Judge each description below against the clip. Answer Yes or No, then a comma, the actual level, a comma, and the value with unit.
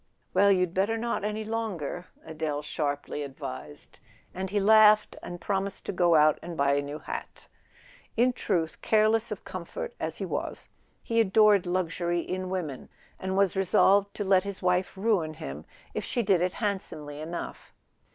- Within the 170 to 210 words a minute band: No, average, 160 wpm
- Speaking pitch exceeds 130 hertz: Yes, medium, 185 Hz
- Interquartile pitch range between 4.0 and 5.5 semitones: Yes, average, 4.6 semitones